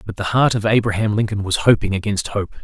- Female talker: No, male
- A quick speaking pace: Yes, fast, 230 wpm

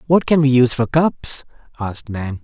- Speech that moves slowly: No, average, 200 wpm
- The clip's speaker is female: No, male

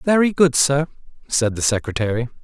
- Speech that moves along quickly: No, average, 150 wpm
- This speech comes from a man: Yes, male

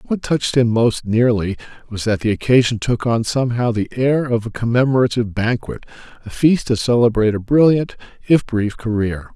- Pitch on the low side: Yes, low, 120 Hz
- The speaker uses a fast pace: No, average, 175 wpm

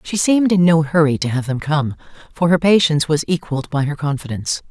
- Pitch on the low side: No, medium, 155 Hz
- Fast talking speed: Yes, fast, 215 wpm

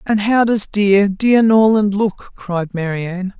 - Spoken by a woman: Yes, female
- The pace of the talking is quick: No, average, 160 wpm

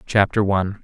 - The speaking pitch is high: No, low, 100 Hz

